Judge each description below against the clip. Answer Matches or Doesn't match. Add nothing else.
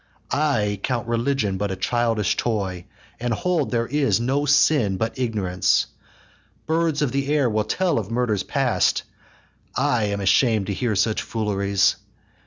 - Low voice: Matches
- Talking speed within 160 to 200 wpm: Doesn't match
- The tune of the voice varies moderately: Matches